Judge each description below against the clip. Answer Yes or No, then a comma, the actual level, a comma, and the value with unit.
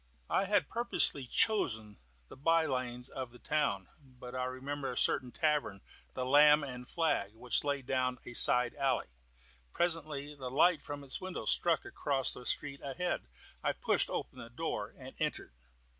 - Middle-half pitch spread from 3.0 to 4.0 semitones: Yes, average, 3.3 semitones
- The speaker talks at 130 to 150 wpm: No, average, 165 wpm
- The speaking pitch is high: No, low, 135 Hz